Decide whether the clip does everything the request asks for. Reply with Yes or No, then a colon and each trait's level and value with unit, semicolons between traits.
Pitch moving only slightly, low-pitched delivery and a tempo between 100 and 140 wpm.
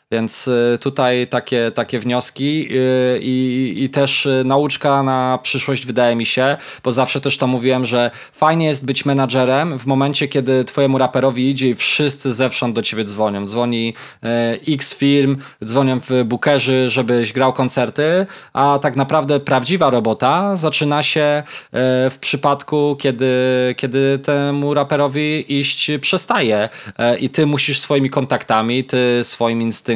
Yes: narrow, 2.2 semitones; low, 130 Hz; average, 135 wpm